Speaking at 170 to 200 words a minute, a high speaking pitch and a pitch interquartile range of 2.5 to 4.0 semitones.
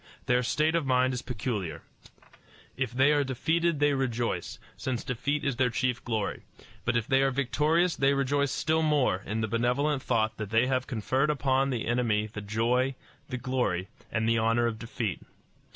No: average, 180 wpm; low, 125 Hz; average, 3.4 semitones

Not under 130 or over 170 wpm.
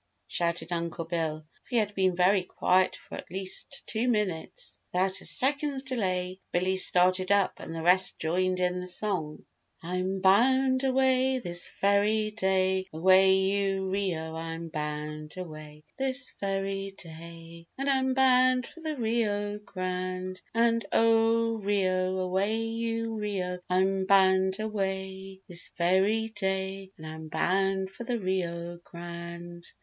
Yes: average, 145 wpm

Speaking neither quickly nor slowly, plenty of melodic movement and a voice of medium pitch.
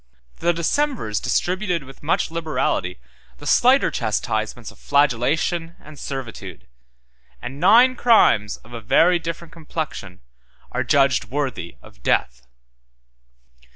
No: slow, 115 wpm; wide, 6.6 semitones; medium, 145 Hz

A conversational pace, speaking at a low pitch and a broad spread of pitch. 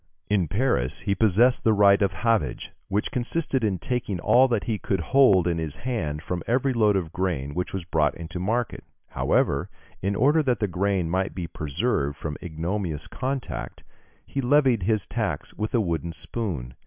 Yes: average, 180 wpm; low, 100 Hz; wide, 6.0 semitones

